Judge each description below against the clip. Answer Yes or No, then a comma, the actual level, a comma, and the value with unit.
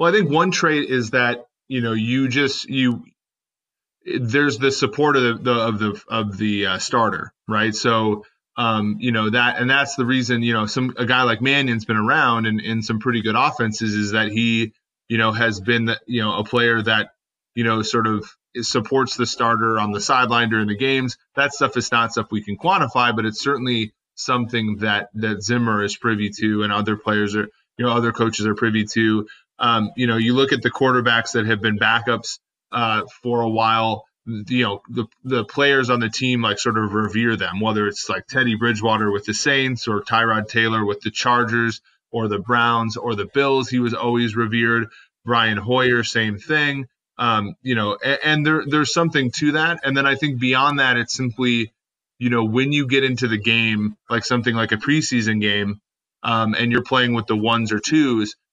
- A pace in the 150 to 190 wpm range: No, fast, 205 wpm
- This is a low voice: Yes, low, 115 Hz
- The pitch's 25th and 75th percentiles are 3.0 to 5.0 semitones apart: No, narrow, 2.5 semitones